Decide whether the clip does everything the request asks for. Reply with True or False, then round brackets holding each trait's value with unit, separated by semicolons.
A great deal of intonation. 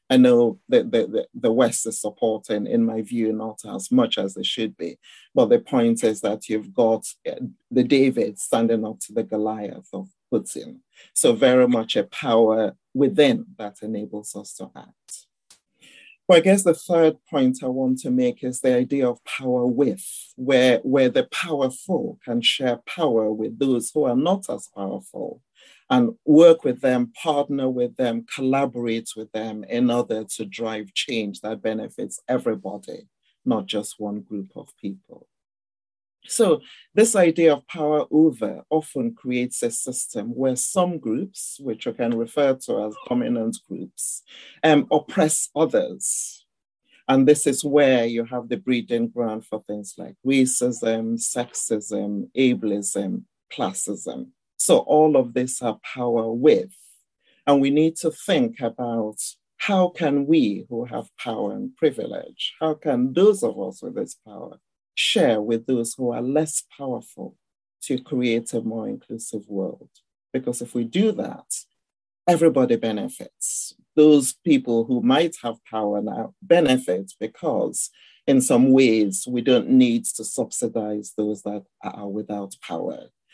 True (6.7 semitones)